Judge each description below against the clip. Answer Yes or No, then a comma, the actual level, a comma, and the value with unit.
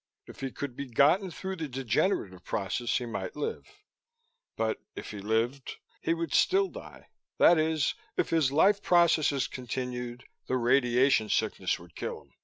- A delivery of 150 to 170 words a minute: Yes, average, 160 wpm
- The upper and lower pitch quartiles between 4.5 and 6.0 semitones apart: Yes, average, 5.3 semitones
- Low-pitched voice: Yes, low, 130 Hz